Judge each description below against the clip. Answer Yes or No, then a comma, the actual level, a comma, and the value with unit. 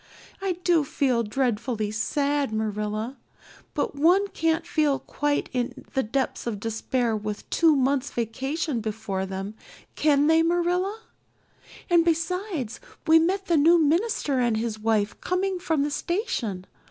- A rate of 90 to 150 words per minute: Yes, average, 140 wpm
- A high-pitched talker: Yes, very high, 280 Hz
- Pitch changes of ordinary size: No, wide, 7.0 semitones